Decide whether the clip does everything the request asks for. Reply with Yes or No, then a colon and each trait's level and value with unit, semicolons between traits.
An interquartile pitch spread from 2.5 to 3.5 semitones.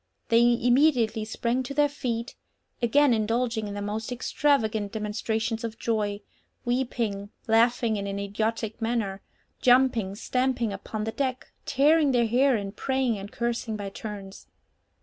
Yes: average, 2.8 semitones